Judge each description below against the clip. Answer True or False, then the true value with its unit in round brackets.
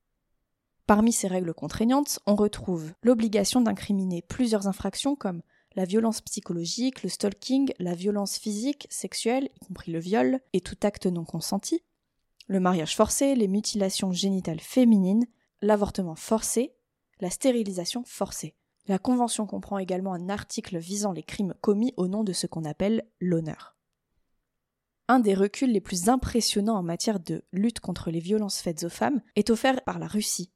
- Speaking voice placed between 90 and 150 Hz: False (205 Hz)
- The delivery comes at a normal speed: True (155 wpm)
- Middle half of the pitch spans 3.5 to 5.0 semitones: True (3.8 semitones)